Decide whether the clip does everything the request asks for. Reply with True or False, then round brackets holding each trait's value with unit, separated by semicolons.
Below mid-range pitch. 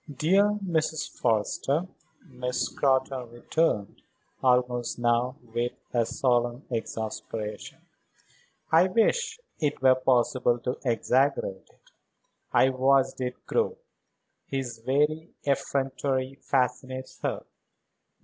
True (130 Hz)